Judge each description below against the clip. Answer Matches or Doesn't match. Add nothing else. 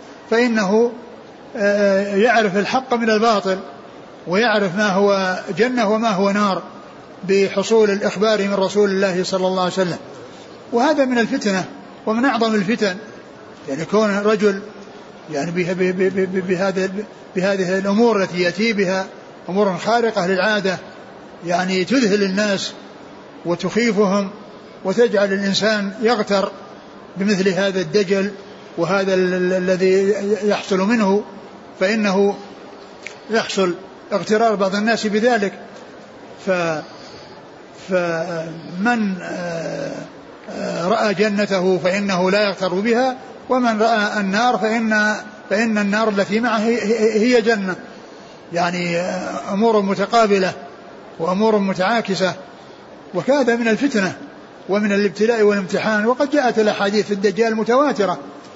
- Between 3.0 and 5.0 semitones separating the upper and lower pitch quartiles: Doesn't match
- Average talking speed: Matches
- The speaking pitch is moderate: Doesn't match